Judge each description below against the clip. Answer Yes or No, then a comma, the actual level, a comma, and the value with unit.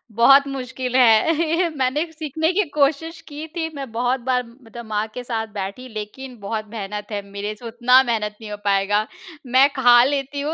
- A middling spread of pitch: Yes, average, 4.4 semitones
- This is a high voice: Yes, very high, 250 Hz